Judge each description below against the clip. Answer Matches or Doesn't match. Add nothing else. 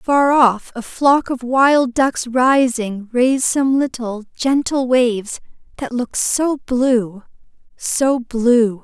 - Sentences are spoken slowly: Matches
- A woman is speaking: Matches